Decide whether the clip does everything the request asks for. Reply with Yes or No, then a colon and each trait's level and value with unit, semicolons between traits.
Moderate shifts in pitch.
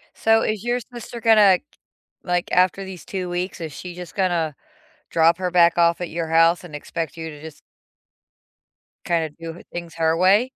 No: narrow, 2.3 semitones